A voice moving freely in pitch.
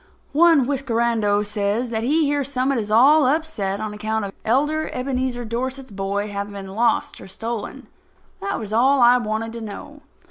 No: average, 4.5 semitones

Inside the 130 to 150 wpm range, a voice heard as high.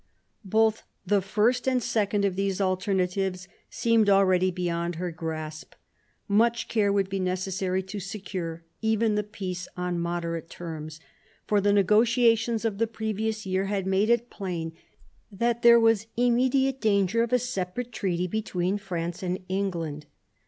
Yes: average, 145 wpm; high, 195 Hz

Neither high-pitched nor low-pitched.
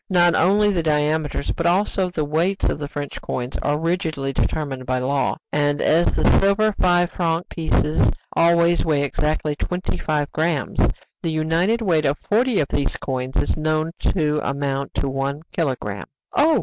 Yes: medium, 155 Hz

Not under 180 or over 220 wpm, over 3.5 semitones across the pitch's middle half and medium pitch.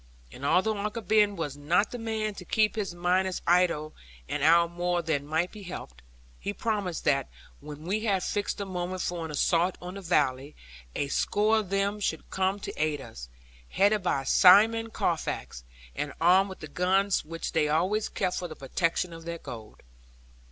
Yes: average, 185 wpm; average, 4.3 semitones; medium, 180 Hz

